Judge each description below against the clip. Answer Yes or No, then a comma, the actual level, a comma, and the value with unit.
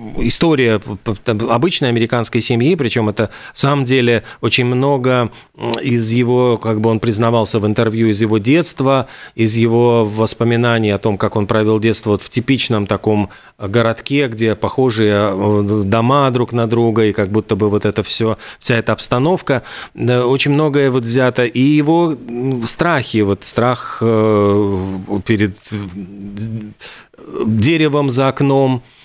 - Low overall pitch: Yes, low, 115 Hz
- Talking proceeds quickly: No, average, 135 wpm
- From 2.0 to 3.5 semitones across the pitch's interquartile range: Yes, average, 2.8 semitones